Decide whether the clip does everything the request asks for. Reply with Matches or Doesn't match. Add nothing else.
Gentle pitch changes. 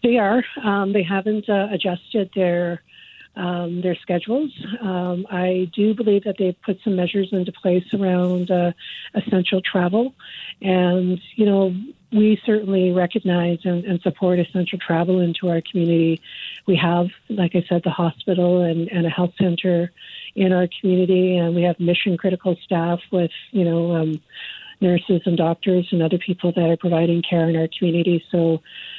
Matches